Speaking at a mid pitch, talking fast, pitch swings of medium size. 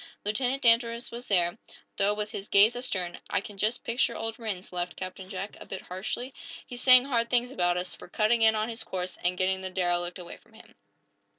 No: high, 210 Hz; fast, 210 wpm; average, 4.2 semitones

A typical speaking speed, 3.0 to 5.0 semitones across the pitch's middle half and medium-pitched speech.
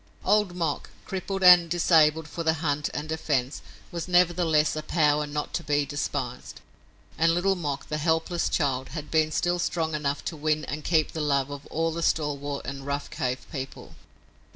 No: average, 175 wpm; narrow, 2.6 semitones; medium, 155 Hz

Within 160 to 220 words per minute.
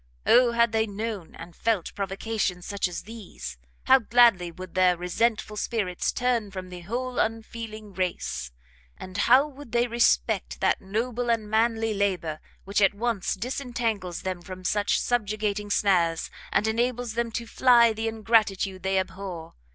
No: average, 150 wpm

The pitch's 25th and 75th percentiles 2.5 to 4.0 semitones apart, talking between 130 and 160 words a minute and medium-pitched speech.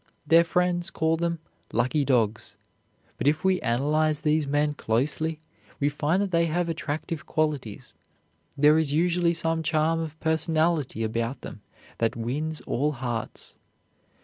Yes: average, 2.8 semitones; average, 140 wpm; medium, 155 Hz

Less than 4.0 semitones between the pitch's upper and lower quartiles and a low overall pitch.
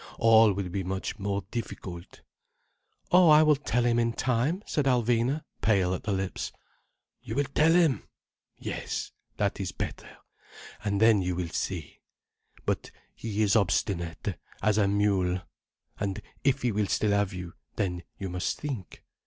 No: average, 4.4 semitones; low, 105 Hz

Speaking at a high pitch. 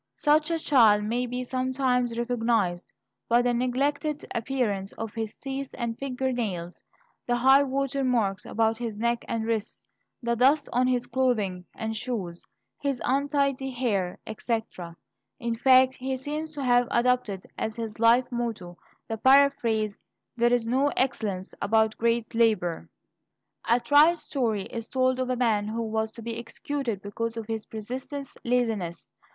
Yes: high, 240 Hz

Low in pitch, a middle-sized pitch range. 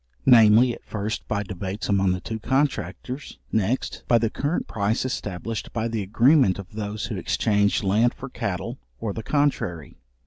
Yes: low, 110 Hz; average, 3.4 semitones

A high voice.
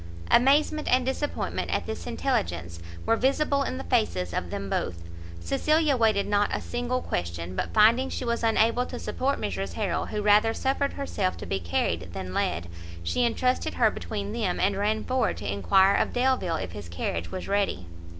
Yes: high, 210 Hz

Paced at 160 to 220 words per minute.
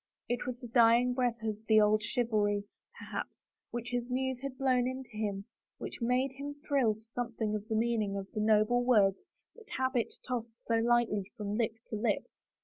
Yes: average, 190 wpm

